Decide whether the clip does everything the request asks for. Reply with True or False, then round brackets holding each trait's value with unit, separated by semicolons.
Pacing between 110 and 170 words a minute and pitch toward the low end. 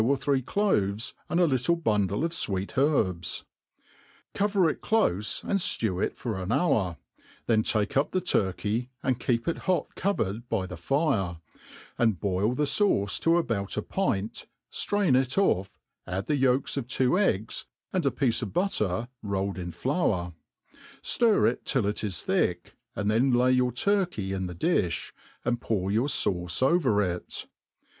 True (165 wpm; 120 Hz)